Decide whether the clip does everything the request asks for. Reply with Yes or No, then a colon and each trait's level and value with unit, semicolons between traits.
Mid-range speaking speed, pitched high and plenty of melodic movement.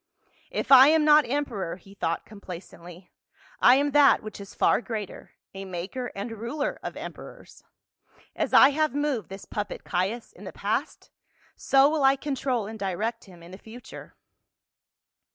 Yes: average, 170 wpm; high, 225 Hz; wide, 6.1 semitones